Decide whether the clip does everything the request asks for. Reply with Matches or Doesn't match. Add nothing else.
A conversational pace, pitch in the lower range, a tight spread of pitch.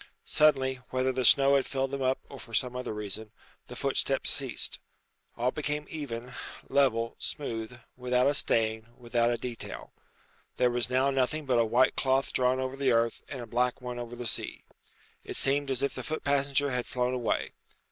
Matches